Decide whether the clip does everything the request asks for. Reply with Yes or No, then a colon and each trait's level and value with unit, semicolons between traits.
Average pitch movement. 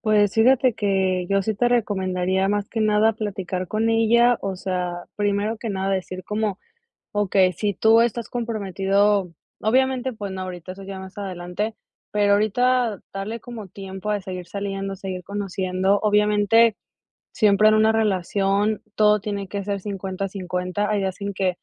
No: narrow, 2.3 semitones